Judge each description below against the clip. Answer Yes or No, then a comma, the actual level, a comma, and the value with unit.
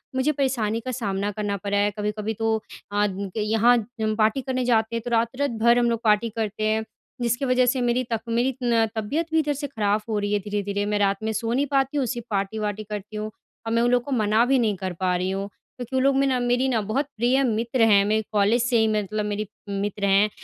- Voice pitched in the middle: No, high, 220 Hz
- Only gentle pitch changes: No, average, 3.0 semitones